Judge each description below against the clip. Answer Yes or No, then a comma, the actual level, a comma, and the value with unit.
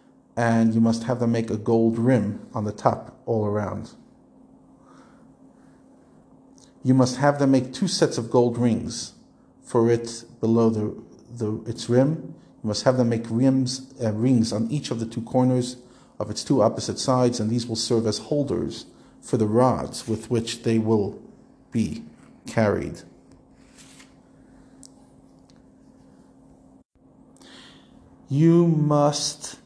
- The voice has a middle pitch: No, low, 120 Hz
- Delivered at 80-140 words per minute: Yes, slow, 135 wpm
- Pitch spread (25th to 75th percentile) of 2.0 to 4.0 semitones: Yes, narrow, 2.5 semitones